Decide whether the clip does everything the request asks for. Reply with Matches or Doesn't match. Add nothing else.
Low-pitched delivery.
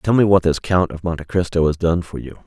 Matches